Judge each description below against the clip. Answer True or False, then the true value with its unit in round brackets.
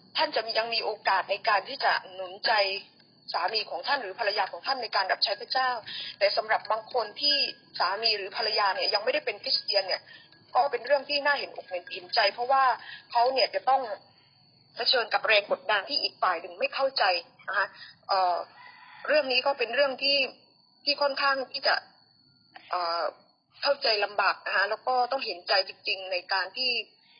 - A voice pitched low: False (245 Hz)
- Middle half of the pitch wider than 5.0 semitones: True (5.5 semitones)